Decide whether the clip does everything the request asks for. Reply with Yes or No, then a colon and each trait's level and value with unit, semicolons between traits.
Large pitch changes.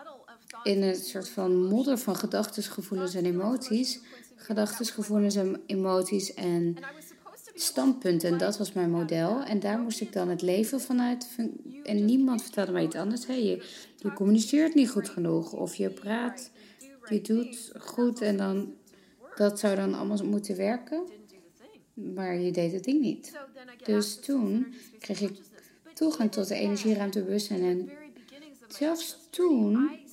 No: average, 4.4 semitones